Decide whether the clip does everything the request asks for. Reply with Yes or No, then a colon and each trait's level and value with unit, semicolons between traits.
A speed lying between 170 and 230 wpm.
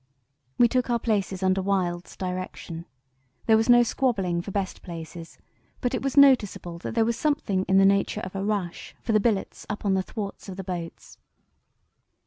Yes: average, 185 wpm